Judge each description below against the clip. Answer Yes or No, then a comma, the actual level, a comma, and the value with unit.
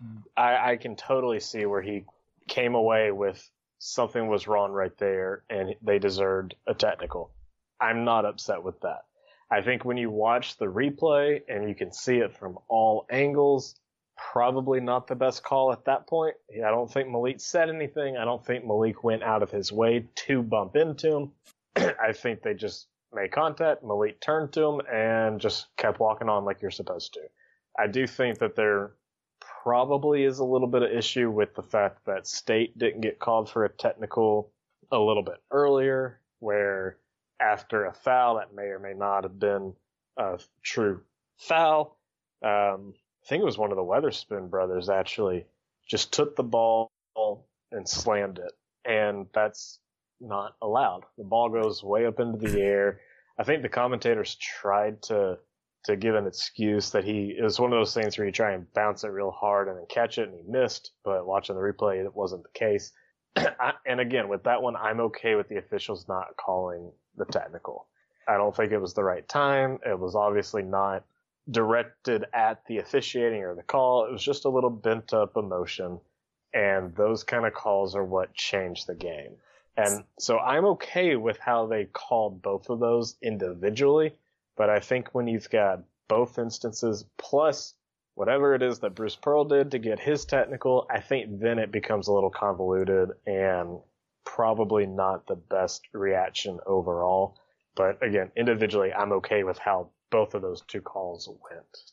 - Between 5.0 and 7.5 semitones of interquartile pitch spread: No, average, 4.5 semitones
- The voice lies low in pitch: Yes, low, 110 Hz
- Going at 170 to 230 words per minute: Yes, average, 180 wpm